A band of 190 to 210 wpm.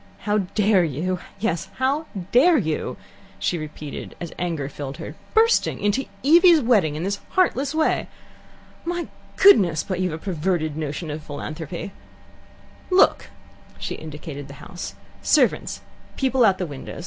No: average, 150 wpm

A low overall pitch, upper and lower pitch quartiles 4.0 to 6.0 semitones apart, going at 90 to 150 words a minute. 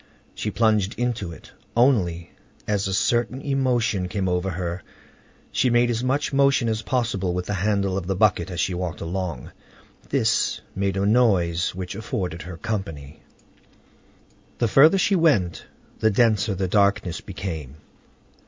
Yes: low, 100 Hz; average, 4.7 semitones; average, 145 wpm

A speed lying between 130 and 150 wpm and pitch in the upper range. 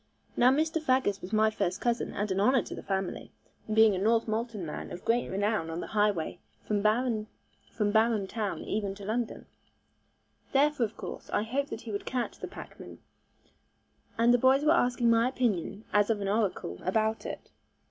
No: average, 180 wpm; high, 220 Hz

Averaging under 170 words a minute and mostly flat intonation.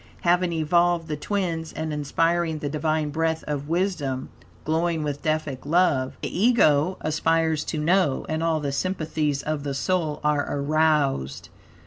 Yes: average, 145 wpm; narrow, 2.3 semitones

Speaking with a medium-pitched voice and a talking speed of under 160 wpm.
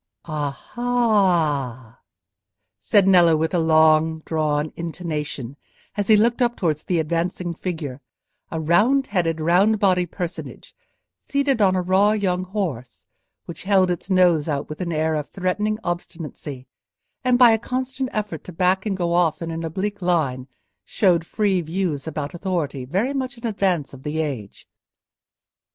Yes: medium, 175 Hz; average, 150 wpm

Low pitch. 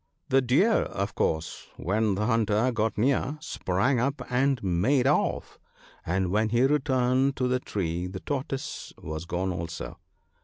Yes: low, 115 Hz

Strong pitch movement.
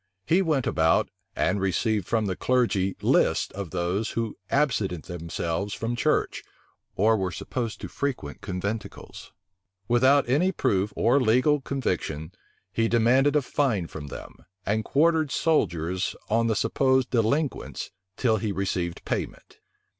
Yes: wide, 5.9 semitones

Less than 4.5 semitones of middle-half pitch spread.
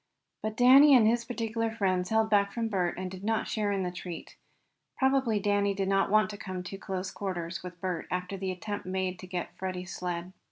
Yes: average, 3.0 semitones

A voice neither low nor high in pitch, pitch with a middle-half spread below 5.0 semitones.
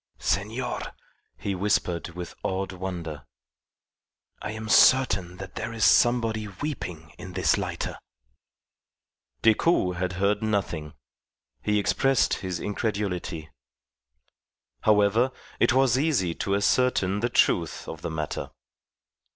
No: low, 100 Hz; average, 3.8 semitones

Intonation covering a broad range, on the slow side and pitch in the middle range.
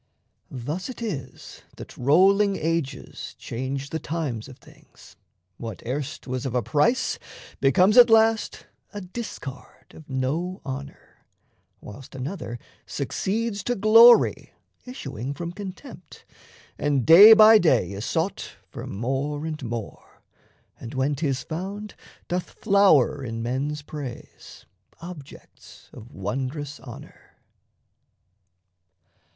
Yes: wide, 6.8 semitones; slow, 115 wpm; medium, 150 Hz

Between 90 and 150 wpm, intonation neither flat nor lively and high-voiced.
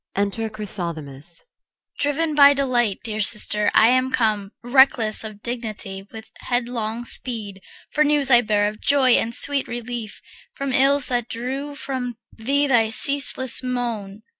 Yes: average, 145 wpm; average, 3.7 semitones; high, 240 Hz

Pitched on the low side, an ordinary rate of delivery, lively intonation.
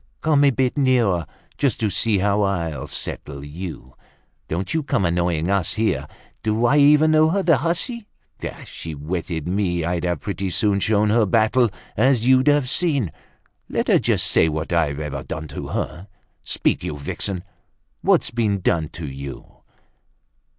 Yes: low, 100 Hz; average, 165 wpm; wide, 7.6 semitones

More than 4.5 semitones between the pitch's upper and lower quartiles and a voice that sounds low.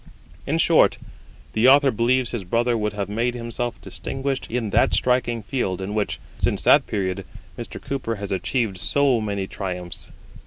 No: average, 3.8 semitones; low, 115 Hz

